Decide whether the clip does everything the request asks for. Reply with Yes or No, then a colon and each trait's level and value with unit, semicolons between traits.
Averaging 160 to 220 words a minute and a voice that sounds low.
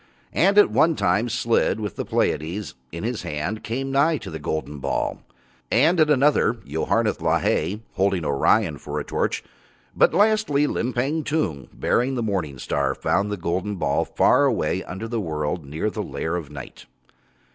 Yes: average, 170 wpm; low, 105 Hz